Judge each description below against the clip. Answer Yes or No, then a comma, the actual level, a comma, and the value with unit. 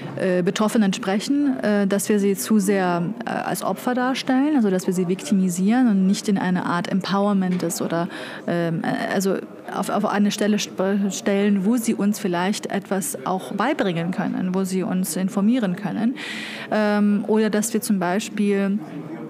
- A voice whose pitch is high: Yes, high, 200 Hz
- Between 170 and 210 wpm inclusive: No, average, 145 wpm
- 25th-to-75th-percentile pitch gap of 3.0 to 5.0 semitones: No, narrow, 2.5 semitones